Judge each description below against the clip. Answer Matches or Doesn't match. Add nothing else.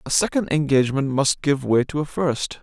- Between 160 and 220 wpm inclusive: Matches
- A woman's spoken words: Doesn't match